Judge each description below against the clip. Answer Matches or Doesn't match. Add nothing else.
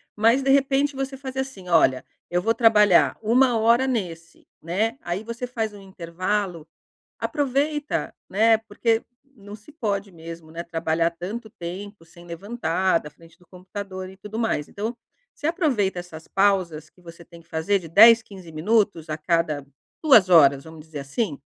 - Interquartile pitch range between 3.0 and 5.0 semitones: Doesn't match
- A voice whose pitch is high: Matches